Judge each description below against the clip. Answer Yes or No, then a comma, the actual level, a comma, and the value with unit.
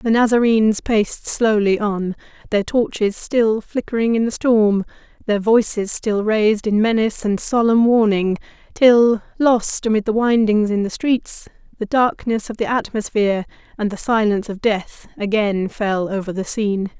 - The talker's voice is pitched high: Yes, high, 215 Hz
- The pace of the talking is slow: No, average, 155 wpm